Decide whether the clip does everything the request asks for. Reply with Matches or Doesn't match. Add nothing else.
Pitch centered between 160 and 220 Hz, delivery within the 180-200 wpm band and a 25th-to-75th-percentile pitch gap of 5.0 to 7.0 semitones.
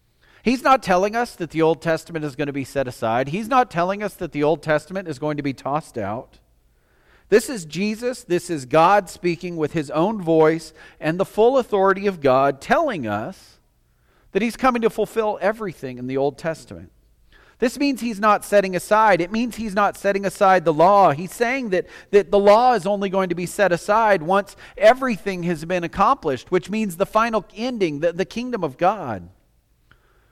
Matches